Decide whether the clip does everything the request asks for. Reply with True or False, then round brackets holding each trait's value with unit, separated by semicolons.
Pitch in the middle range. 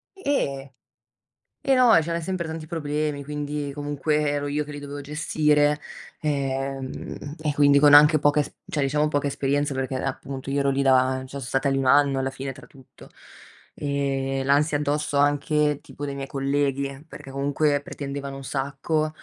True (145 Hz)